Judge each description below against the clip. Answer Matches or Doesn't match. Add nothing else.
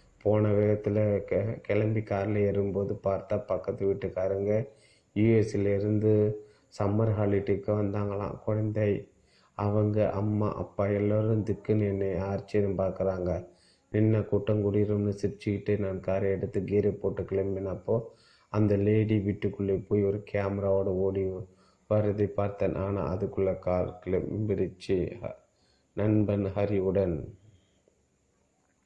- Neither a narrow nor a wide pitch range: Doesn't match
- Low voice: Matches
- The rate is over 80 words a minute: Matches